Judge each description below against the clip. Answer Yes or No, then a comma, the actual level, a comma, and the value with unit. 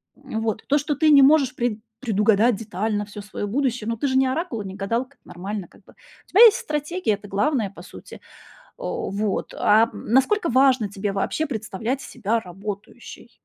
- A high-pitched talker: Yes, high, 225 Hz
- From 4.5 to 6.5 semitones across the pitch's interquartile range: Yes, average, 5.1 semitones